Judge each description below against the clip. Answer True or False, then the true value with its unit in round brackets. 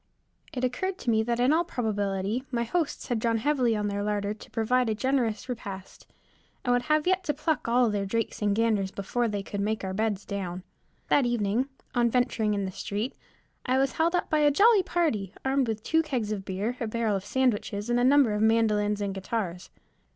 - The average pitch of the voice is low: False (230 Hz)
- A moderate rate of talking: False (210 wpm)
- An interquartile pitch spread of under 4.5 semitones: True (4.0 semitones)